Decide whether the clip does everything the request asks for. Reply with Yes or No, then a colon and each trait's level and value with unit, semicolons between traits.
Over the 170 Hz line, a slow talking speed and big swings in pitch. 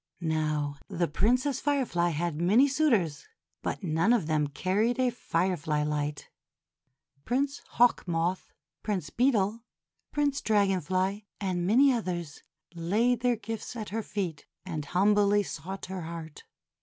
Yes: high, 190 Hz; slow, 130 wpm; wide, 5.8 semitones